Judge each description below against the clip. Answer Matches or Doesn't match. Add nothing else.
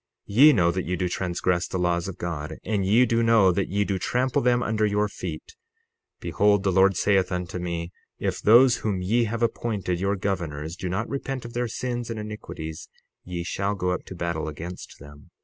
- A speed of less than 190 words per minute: Doesn't match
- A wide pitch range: Doesn't match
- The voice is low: Matches